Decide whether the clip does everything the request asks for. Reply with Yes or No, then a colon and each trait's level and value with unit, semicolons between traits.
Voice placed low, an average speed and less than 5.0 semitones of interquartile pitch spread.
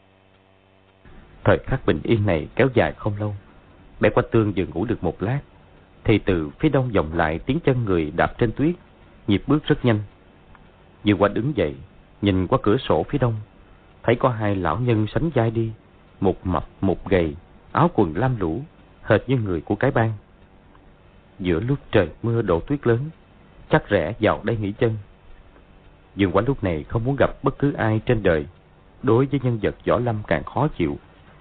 Yes: low, 100 Hz; average, 190 wpm; average, 3.5 semitones